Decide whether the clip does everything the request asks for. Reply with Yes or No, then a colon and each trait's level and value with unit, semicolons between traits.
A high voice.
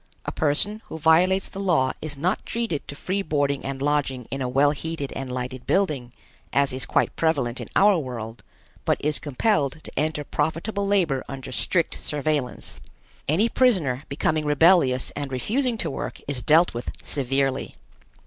No: medium, 145 Hz